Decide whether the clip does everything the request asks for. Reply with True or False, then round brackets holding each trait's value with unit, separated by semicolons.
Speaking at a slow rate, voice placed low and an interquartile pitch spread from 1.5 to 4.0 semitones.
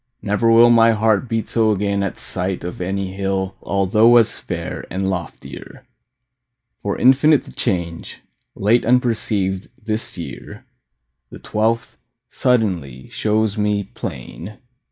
True (125 wpm; 105 Hz; 3.1 semitones)